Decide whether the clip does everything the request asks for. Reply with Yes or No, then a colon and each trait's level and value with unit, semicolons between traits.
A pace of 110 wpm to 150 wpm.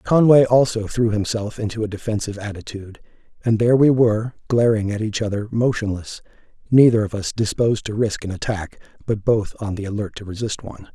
No: average, 180 wpm